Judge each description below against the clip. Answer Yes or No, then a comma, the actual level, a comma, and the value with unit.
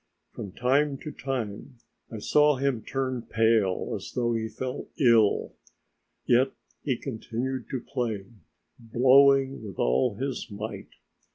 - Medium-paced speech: No, slow, 125 wpm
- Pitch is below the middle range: Yes, low, 125 Hz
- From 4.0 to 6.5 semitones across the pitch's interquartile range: No, average, 3.3 semitones